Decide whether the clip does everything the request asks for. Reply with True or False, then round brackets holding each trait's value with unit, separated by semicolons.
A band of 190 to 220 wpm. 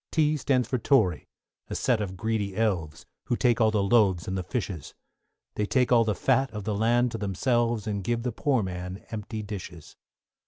True (195 wpm)